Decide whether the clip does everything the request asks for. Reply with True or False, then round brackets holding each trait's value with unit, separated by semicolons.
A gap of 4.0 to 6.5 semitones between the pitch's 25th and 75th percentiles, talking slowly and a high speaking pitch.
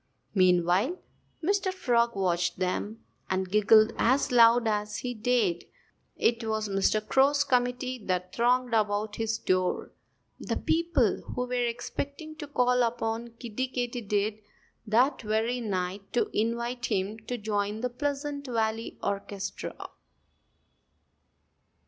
False (3.2 semitones; 120 wpm; 230 Hz)